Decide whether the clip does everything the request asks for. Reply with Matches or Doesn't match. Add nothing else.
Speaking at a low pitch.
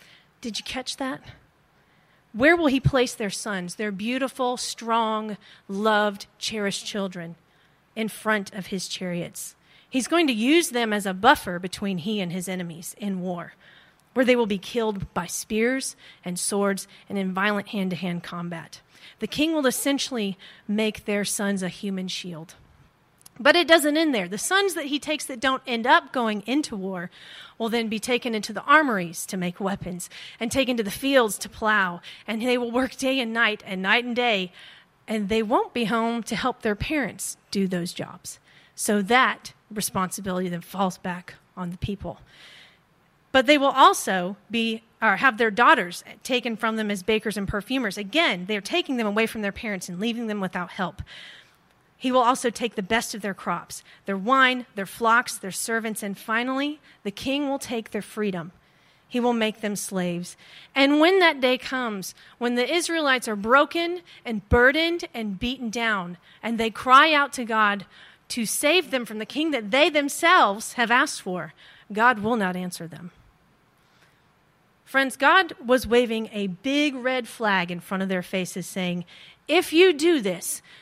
Doesn't match